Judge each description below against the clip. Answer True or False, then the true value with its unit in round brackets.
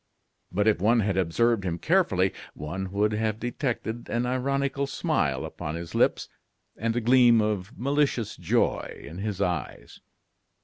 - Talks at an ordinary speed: True (145 wpm)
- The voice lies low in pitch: True (110 Hz)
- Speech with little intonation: False (4.5 semitones)